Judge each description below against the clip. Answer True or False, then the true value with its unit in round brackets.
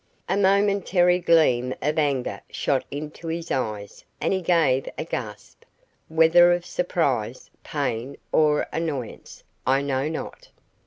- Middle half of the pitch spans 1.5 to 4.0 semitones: False (4.8 semitones)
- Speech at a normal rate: False (125 wpm)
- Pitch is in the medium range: True (155 Hz)